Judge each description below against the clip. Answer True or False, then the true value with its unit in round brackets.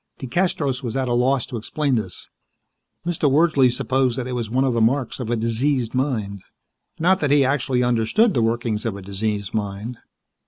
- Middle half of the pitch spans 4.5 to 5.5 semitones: False (3.4 semitones)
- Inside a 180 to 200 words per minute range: True (190 wpm)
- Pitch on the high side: False (125 Hz)